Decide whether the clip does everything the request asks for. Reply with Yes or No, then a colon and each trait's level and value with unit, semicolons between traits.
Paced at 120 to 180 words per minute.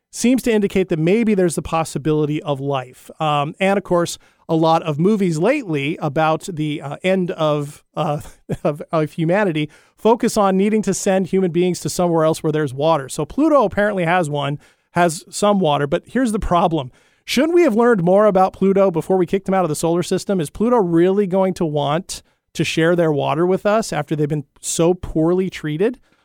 No: average, 200 wpm